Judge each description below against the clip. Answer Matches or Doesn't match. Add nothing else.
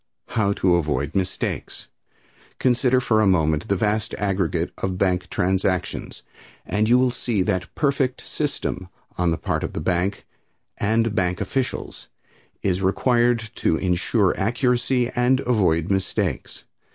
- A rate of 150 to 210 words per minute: Doesn't match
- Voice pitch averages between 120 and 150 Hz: Doesn't match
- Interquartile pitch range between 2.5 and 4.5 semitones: Doesn't match